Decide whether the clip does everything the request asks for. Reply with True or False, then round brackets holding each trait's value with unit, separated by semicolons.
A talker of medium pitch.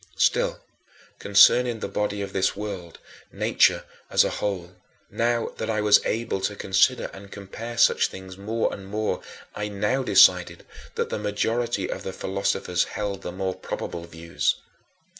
False (100 Hz)